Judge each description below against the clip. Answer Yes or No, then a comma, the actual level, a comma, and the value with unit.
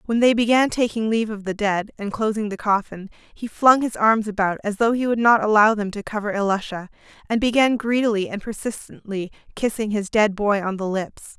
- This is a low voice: No, high, 215 Hz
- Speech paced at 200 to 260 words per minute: Yes, fast, 205 wpm